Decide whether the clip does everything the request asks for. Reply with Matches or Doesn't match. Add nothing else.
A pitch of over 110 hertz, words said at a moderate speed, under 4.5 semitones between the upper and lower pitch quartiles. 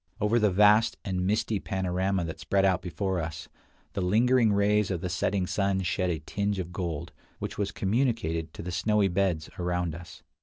Doesn't match